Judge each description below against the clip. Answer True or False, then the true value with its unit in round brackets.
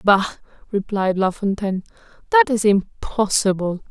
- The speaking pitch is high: True (205 Hz)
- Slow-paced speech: True (110 wpm)